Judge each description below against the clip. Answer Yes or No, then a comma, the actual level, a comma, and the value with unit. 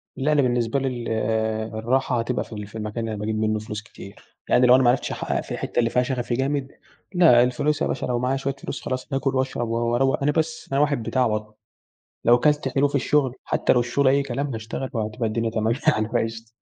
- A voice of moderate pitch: No, low, 125 Hz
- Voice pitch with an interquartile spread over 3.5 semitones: No, average, 3.1 semitones